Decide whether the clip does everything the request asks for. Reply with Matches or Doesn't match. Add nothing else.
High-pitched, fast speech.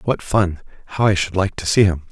Doesn't match